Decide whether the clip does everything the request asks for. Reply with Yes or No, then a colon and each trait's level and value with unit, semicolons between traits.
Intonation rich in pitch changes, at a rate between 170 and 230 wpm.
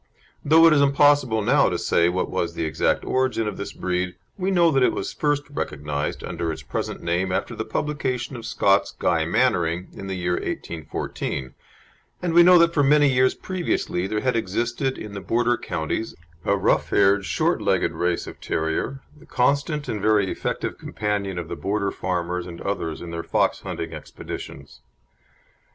Yes: wide, 7.6 semitones; average, 180 wpm